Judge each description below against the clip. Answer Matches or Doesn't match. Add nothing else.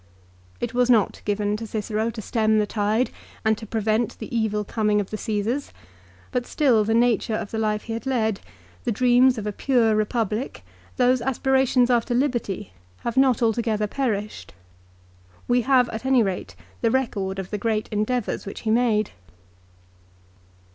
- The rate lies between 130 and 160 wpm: Doesn't match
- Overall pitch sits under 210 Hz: Doesn't match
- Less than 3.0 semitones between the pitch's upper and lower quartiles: Matches